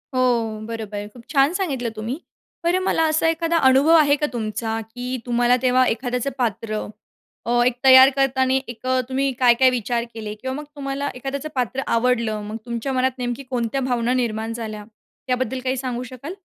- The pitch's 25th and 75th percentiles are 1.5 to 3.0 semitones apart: Yes, narrow, 2.6 semitones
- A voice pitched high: Yes, very high, 250 Hz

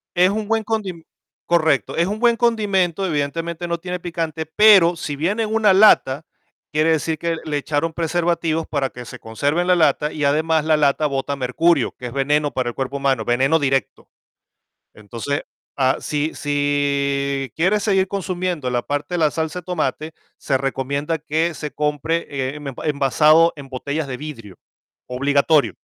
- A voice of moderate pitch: Yes, medium, 155 Hz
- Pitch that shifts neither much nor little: Yes, average, 3.5 semitones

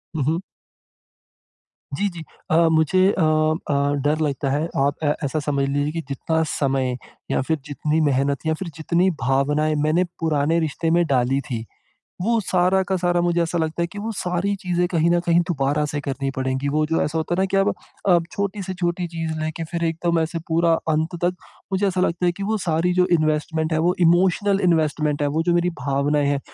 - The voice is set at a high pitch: No, medium, 160 Hz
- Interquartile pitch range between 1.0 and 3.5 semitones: Yes, average, 3.2 semitones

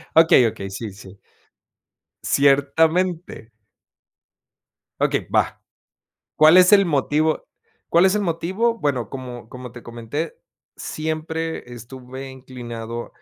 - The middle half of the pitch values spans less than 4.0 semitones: No, average, 5.2 semitones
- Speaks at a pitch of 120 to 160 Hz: Yes, medium, 140 Hz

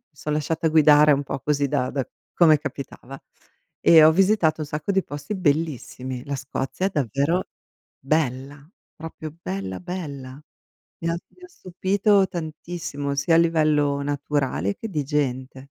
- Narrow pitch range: No, average, 3.1 semitones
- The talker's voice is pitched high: No, medium, 150 Hz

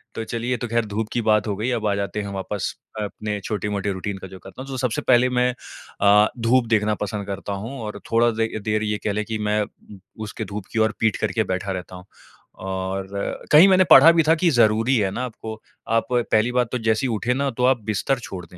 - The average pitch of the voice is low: Yes, low, 110 Hz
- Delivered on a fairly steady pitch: No, average, 3.1 semitones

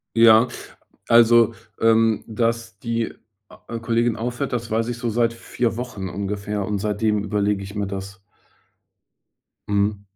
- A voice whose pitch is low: Yes, low, 110 Hz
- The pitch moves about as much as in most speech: No, narrow, 2.3 semitones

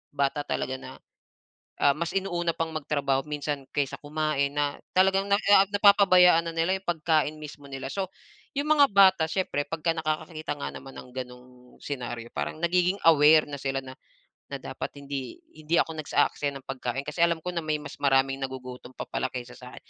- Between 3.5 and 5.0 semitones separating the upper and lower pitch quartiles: Yes, average, 3.8 semitones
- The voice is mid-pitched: Yes, medium, 150 Hz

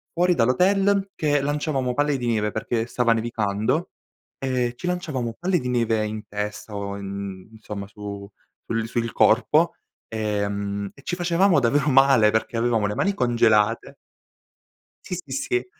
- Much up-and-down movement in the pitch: Yes, wide, 5.7 semitones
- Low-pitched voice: Yes, low, 120 Hz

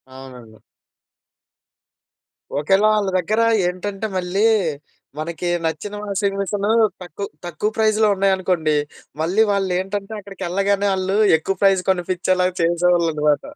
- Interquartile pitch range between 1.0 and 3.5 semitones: Yes, average, 2.7 semitones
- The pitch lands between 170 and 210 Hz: Yes, high, 190 Hz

